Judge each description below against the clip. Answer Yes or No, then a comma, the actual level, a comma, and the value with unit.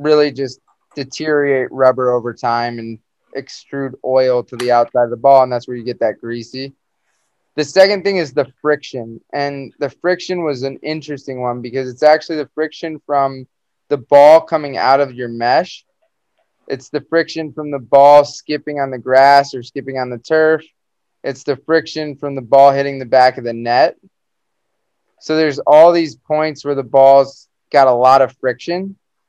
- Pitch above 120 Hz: Yes, medium, 140 Hz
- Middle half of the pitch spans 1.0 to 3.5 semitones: Yes, average, 2.9 semitones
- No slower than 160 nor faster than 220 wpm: Yes, average, 180 wpm